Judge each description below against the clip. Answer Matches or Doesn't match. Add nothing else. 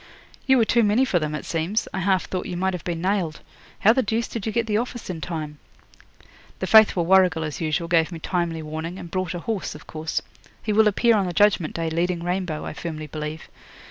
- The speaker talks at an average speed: Doesn't match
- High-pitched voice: Doesn't match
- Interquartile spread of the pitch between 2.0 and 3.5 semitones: Doesn't match